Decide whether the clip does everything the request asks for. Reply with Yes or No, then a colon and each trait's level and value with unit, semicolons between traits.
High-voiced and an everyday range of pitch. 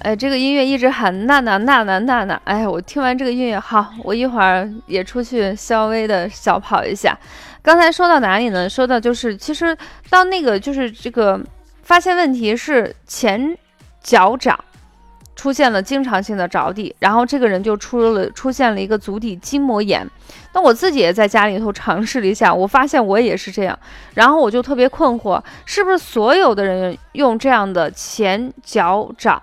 Yes: high, 235 Hz; average, 4.9 semitones